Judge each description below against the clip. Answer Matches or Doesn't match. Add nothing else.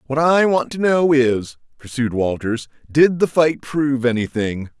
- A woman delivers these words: Doesn't match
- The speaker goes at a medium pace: Matches